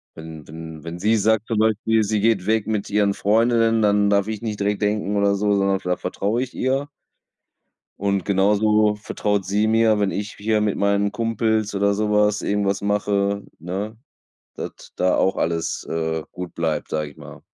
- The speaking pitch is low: Yes, low, 105 Hz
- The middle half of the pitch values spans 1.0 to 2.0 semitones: Yes, narrow, 1.7 semitones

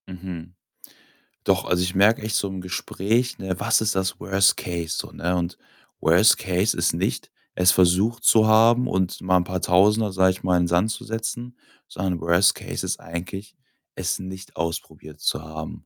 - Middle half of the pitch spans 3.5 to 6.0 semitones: No, average, 2.9 semitones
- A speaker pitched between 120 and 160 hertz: No, very low, 95 Hz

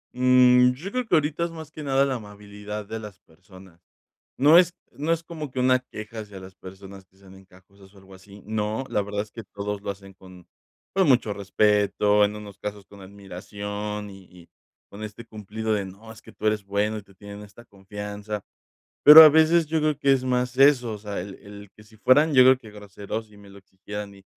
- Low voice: Yes, low, 105 Hz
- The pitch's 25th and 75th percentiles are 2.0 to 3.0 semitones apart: No, average, 4.1 semitones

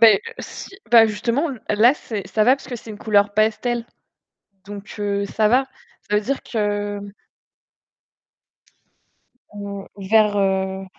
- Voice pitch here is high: Yes, high, 210 Hz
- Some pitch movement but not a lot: No, narrow, 2.2 semitones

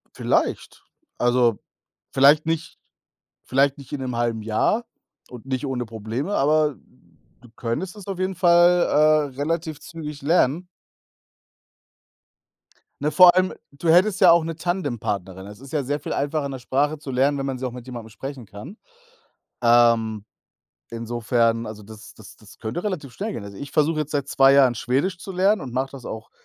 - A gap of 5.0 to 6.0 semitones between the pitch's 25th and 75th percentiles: Yes, wide, 5.5 semitones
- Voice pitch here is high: No, low, 135 Hz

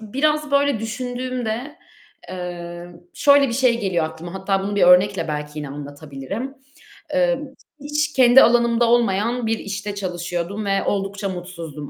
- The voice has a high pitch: Yes, high, 205 Hz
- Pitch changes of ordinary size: No, wide, 5.9 semitones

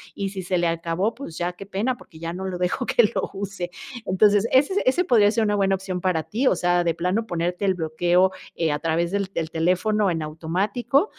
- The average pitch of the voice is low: No, medium, 185 Hz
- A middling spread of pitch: Yes, average, 3.3 semitones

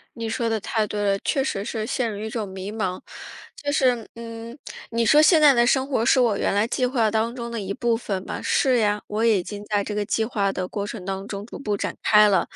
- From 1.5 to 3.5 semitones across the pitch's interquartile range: Yes, narrow, 2.6 semitones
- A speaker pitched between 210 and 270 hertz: Yes, high, 220 Hz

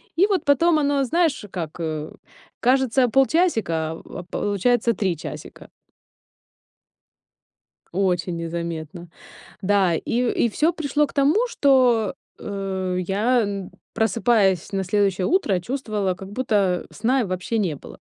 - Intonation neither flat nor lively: No, wide, 6.4 semitones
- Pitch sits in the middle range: No, high, 205 Hz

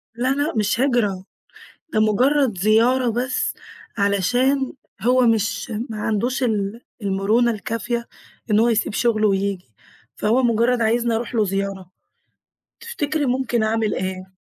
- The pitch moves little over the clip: No, average, 3.4 semitones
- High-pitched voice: Yes, high, 225 Hz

